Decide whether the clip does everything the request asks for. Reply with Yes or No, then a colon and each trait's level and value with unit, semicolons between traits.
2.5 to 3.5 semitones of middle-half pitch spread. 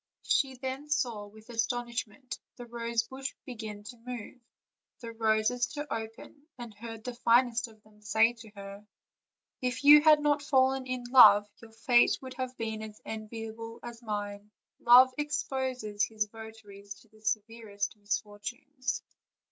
Yes: average, 2.8 semitones